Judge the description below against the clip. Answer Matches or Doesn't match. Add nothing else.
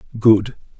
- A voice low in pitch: Matches